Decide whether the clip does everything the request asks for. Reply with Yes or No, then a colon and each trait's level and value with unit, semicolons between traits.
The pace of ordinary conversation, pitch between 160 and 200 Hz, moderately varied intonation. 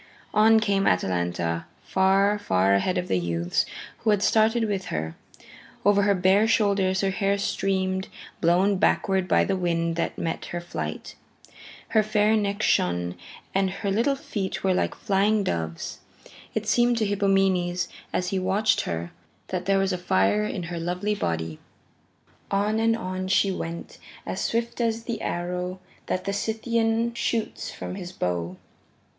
Yes: average, 155 wpm; high, 190 Hz; average, 3.3 semitones